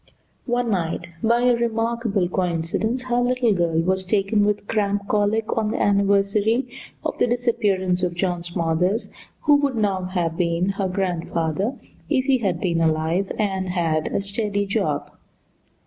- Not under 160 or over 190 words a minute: No, average, 150 wpm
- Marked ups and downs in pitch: No, average, 4.1 semitones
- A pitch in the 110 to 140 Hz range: No, high, 200 Hz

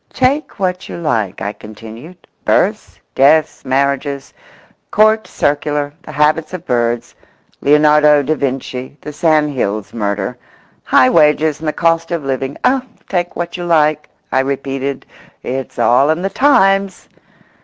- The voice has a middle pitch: Yes, medium, 150 Hz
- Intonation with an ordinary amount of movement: Yes, average, 4.1 semitones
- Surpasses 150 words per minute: No, slow, 135 wpm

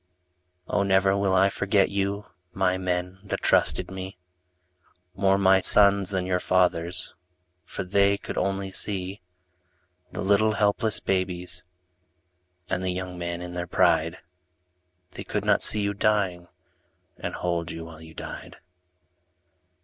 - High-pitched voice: No, very low, 95 Hz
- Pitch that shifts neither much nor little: No, narrow, 1.9 semitones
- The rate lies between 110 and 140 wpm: Yes, slow, 135 wpm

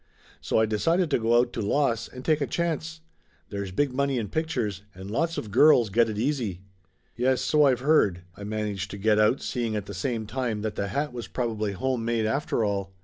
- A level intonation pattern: No, average, 4.7 semitones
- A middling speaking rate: No, fast, 225 wpm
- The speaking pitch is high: No, low, 115 Hz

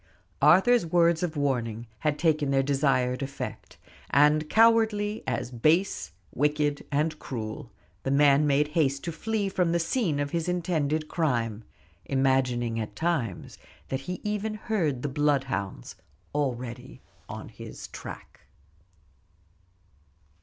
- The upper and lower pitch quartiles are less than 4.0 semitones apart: No, average, 4.3 semitones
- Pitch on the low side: No, medium, 145 Hz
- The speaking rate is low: Yes, slow, 125 wpm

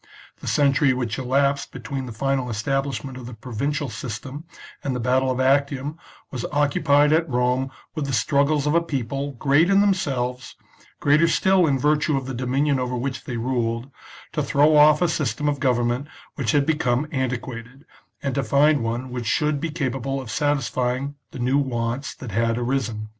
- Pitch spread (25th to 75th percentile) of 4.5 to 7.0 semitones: No, average, 2.8 semitones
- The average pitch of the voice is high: No, low, 135 Hz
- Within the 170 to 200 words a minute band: Yes, average, 180 wpm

